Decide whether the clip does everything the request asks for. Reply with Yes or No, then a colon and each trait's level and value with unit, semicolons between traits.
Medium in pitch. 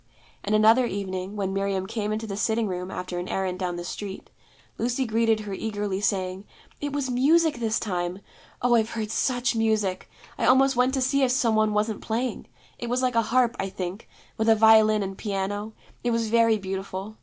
No: high, 215 Hz